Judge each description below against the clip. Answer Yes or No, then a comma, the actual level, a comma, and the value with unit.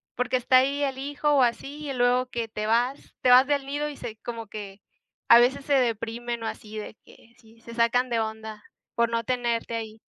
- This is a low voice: No, high, 240 Hz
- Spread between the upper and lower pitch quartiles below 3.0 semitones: Yes, narrow, 2.6 semitones